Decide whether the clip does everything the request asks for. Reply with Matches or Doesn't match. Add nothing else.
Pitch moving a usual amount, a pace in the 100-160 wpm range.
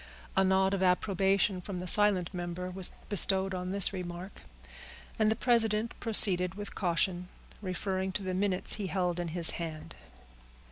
Doesn't match